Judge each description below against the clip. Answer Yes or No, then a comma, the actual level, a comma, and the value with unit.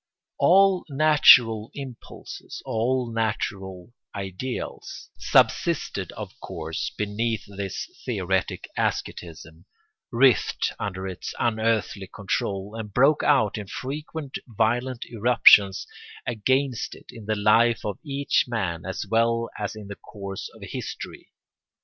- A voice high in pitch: No, low, 110 Hz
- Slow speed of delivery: Yes, slow, 115 wpm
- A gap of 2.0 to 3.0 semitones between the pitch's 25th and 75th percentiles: No, average, 3.9 semitones